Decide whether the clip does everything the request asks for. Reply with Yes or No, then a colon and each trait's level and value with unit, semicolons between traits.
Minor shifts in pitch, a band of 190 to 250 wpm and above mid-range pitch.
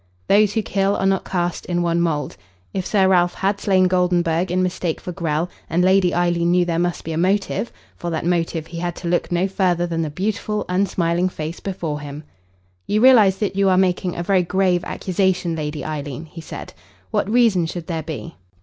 No: narrow, 2.3 semitones; fast, 205 wpm; medium, 175 Hz